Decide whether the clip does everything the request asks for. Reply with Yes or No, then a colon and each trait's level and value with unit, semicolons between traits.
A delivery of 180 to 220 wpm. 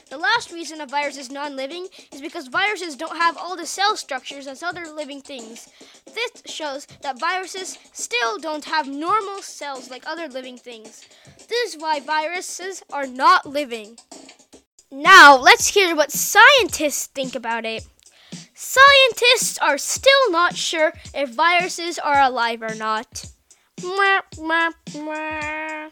No: average, 140 wpm